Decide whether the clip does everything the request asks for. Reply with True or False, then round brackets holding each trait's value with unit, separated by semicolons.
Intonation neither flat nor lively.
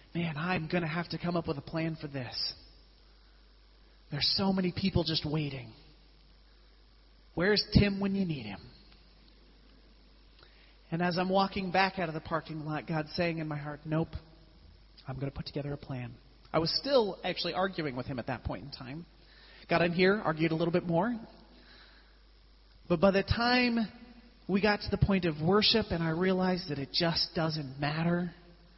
True (4.0 semitones)